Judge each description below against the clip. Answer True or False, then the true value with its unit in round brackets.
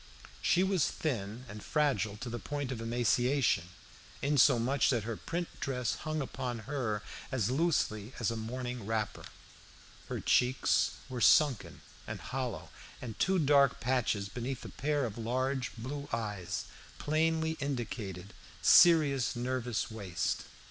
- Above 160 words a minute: False (135 wpm)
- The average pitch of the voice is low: True (125 Hz)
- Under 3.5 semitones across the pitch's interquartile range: False (4.1 semitones)